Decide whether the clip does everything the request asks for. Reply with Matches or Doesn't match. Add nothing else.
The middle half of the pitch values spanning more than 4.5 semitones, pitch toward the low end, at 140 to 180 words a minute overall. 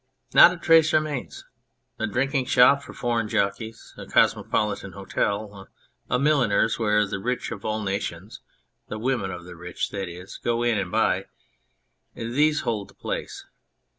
Matches